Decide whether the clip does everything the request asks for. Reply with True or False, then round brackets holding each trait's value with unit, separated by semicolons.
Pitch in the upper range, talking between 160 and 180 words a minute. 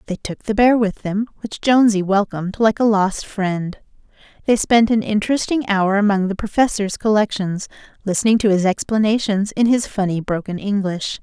True (205 Hz; 165 wpm)